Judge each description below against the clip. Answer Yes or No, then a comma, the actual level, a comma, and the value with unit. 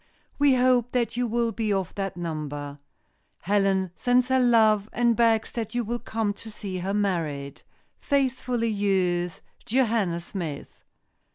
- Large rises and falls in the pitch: No, average, 4.7 semitones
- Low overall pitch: No, high, 210 Hz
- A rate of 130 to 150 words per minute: Yes, average, 145 wpm